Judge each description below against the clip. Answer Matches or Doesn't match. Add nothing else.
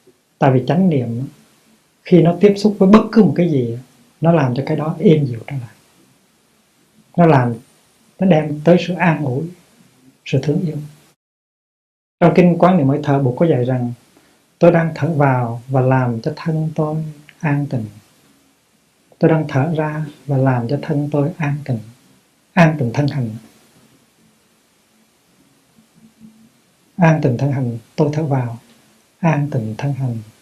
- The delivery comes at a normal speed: Doesn't match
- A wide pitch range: Doesn't match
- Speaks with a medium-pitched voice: Matches